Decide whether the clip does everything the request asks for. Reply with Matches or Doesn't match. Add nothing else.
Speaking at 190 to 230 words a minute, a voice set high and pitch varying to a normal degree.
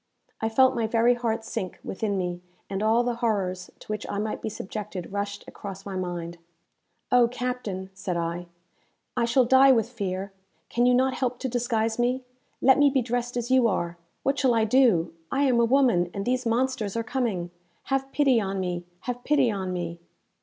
Matches